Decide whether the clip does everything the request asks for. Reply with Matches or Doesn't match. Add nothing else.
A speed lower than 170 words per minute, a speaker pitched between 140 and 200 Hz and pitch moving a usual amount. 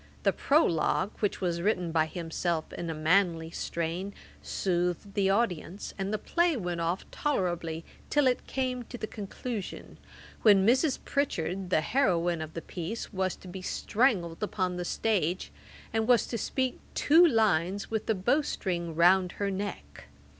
Matches